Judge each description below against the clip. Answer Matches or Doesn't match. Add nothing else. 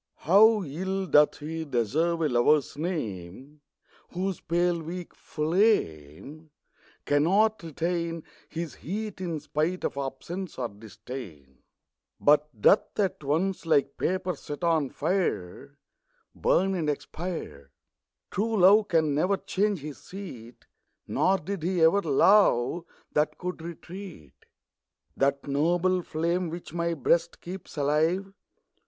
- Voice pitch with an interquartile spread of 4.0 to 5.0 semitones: Matches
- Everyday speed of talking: Doesn't match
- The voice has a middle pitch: Matches